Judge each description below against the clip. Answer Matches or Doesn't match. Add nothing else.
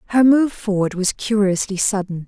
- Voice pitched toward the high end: Matches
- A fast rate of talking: Doesn't match